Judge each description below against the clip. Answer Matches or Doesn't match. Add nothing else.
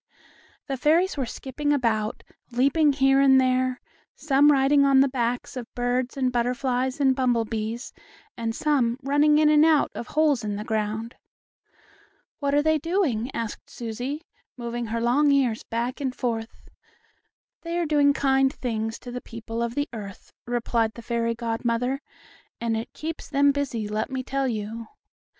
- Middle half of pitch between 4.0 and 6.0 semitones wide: Doesn't match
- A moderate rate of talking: Matches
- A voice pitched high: Matches